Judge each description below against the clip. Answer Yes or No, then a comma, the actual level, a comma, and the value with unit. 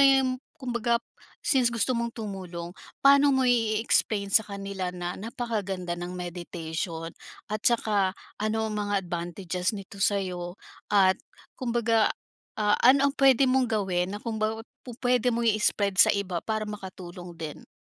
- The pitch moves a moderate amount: Yes, average, 4.3 semitones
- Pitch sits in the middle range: No, high, 210 Hz